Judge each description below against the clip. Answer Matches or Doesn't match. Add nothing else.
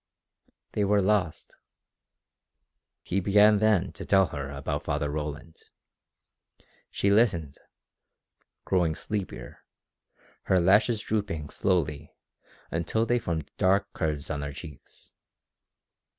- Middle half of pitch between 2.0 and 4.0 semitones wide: Doesn't match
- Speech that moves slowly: Matches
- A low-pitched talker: Matches